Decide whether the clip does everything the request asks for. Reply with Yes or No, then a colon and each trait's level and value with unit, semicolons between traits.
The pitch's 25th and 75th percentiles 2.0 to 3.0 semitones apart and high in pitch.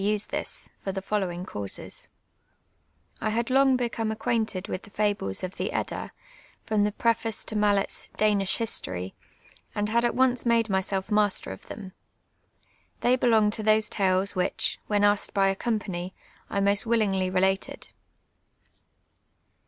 Yes: narrow, 2.6 semitones; high, 205 Hz